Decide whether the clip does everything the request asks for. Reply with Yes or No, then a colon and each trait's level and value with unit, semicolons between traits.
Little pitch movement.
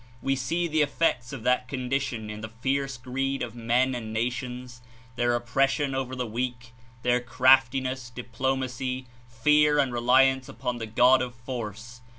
Yes: narrow, 1.7 semitones